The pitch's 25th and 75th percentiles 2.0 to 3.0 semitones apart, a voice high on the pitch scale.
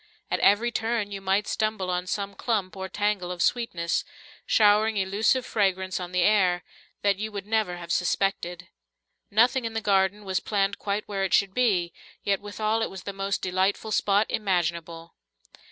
Yes: narrow, 2.5 semitones; high, 200 Hz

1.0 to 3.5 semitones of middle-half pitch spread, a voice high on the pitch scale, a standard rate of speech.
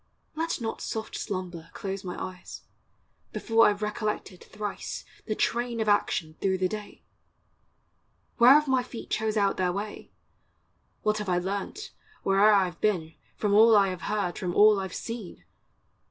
Yes: average, 2.7 semitones; high, 205 Hz; average, 170 wpm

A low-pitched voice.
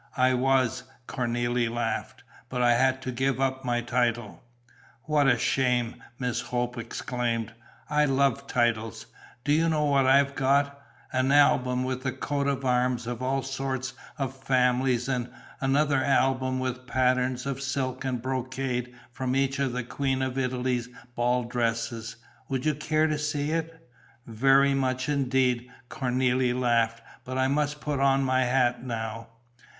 Yes: low, 130 Hz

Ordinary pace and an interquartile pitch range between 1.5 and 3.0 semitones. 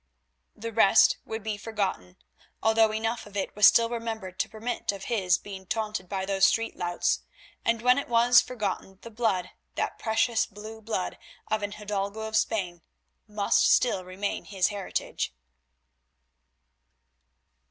Yes: average, 145 wpm; narrow, 2.6 semitones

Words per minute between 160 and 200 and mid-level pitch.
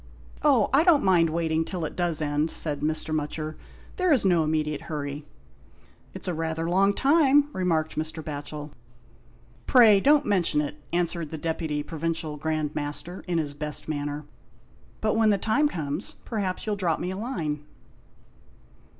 Yes: average, 165 wpm; medium, 165 Hz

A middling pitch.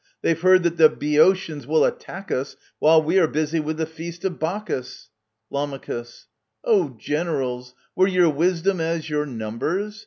Yes: medium, 160 Hz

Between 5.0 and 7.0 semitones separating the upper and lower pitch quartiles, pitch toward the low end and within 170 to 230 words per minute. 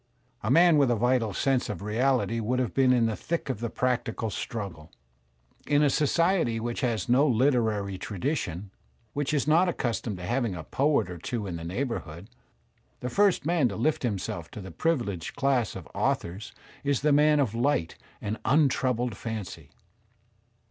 Yes: wide, 5.4 semitones; low, 120 Hz; average, 175 wpm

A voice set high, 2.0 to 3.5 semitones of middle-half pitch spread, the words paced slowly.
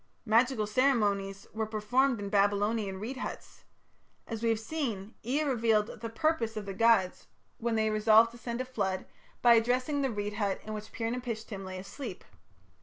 No: high, 225 Hz; average, 2.7 semitones; average, 175 wpm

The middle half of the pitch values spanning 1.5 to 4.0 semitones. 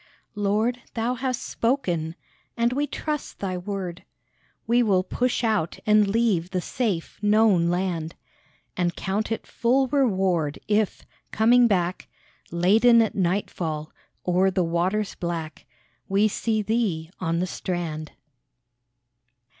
No: average, 4.6 semitones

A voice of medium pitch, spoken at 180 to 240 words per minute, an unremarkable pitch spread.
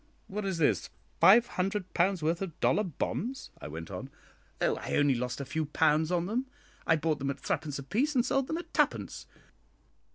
No: medium, 170 Hz; average, 195 wpm; wide, 6.3 semitones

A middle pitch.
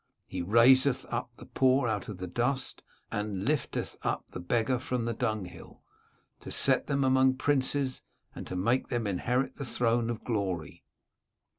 No: low, 120 Hz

